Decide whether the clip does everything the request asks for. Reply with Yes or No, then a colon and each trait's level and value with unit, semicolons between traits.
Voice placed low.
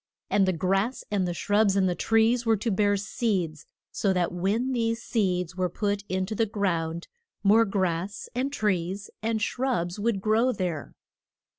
No: high, 200 Hz